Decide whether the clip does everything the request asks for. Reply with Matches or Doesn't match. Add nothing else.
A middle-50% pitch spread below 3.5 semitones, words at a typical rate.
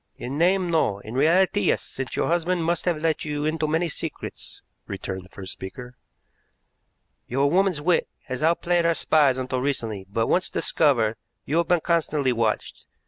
Doesn't match